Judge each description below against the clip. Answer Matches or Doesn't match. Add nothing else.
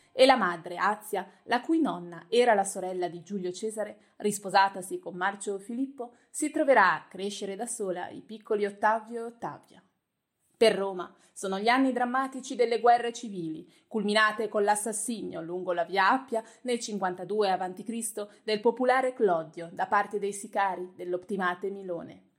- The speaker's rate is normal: Matches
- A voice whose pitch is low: Doesn't match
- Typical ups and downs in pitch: Matches